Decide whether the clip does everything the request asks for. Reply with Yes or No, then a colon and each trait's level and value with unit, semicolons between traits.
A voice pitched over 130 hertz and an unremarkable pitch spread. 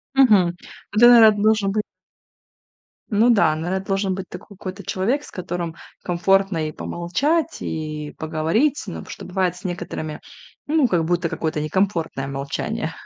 Yes: medium, 185 Hz; average, 4.5 semitones